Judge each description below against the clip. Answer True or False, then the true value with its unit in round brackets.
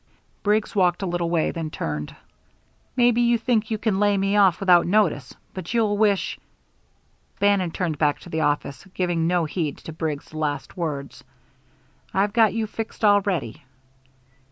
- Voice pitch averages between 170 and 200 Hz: True (185 Hz)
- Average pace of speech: True (160 wpm)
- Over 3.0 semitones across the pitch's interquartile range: True (4.5 semitones)